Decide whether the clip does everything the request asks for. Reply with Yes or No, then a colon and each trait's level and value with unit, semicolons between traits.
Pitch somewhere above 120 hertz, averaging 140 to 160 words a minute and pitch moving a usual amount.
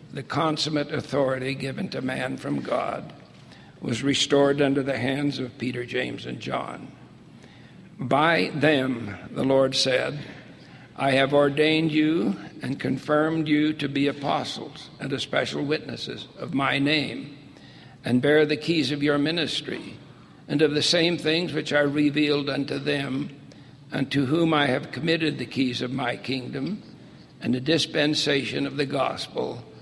No: medium, 140 Hz; average, 145 wpm; narrow, 2.1 semitones